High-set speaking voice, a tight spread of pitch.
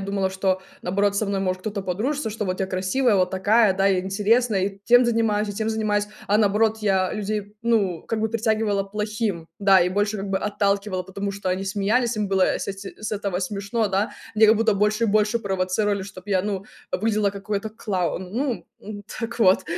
Yes: high, 205 Hz; narrow, 2.0 semitones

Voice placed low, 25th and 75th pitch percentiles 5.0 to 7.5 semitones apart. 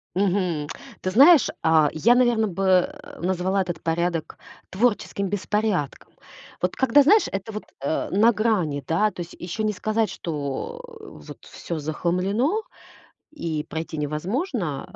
No: high, 190 Hz; wide, 5.4 semitones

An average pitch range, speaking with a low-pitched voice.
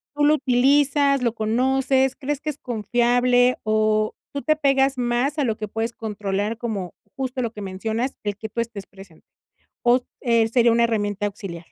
No: average, 3.6 semitones; high, 235 Hz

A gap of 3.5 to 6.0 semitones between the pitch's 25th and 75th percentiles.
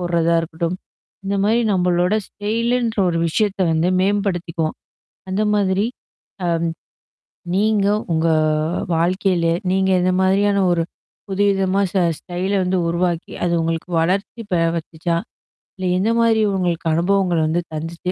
No: average, 2.9 semitones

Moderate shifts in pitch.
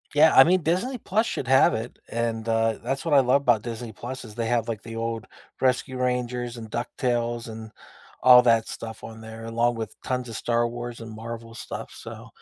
No: narrow, 1.9 semitones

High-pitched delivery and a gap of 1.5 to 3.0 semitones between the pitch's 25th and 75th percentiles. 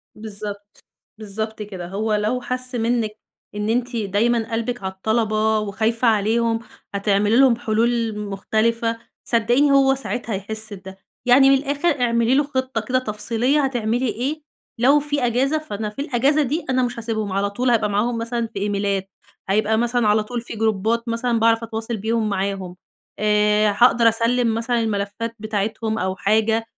Yes: high, 225 Hz; narrow, 2.5 semitones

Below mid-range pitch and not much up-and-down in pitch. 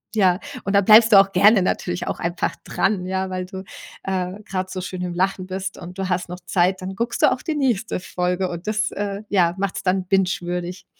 No: high, 190 Hz; narrow, 1.6 semitones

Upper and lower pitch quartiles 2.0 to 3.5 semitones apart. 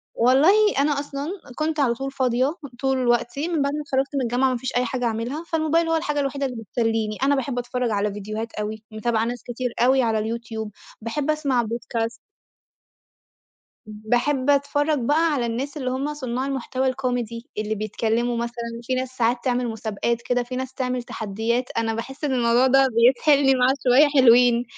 Yes: average, 2.9 semitones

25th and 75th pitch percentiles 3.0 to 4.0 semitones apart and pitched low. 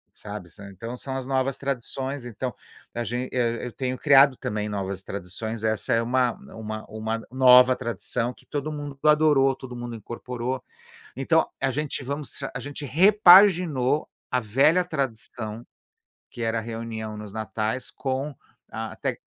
Yes: average, 3.5 semitones; low, 125 Hz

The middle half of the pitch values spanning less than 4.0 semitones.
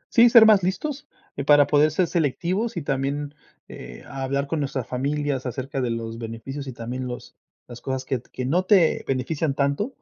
No: average, 4.3 semitones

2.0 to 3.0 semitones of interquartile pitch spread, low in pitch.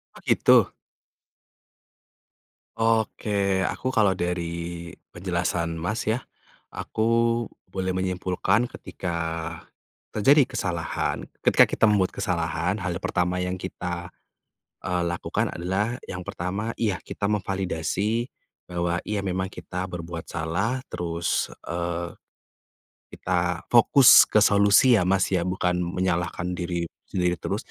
Yes: narrow, 2.6 semitones; very low, 90 Hz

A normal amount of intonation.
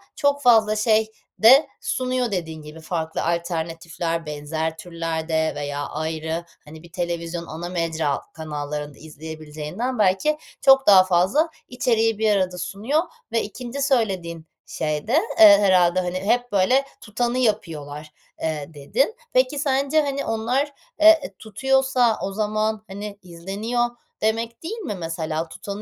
No: wide, 6.7 semitones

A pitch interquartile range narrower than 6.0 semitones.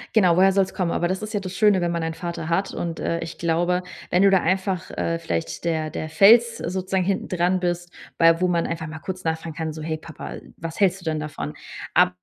Yes: narrow, 2.4 semitones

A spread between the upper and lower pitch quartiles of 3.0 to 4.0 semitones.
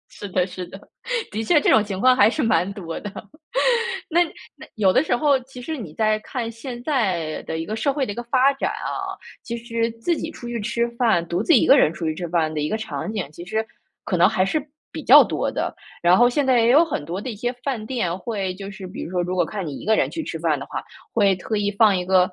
No: average, 5.0 semitones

